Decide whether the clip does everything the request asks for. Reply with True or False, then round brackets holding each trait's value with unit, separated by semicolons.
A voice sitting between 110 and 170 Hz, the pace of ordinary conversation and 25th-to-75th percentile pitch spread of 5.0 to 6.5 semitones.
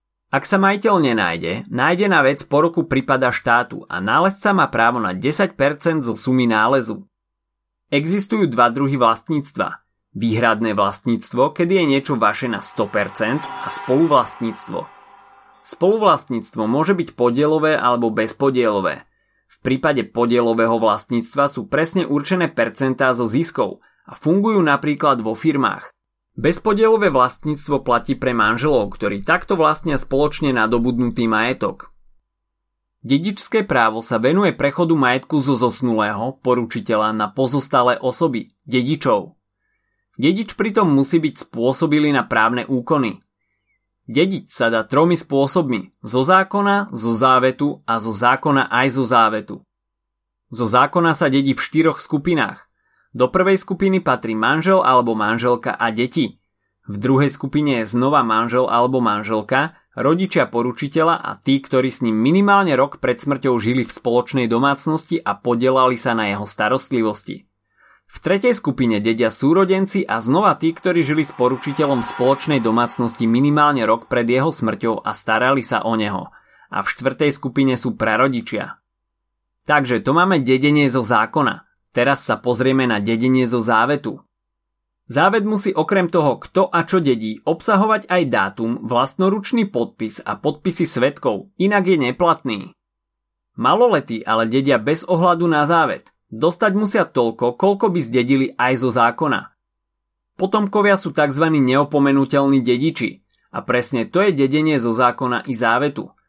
True (130 Hz; 135 wpm; 5.5 semitones)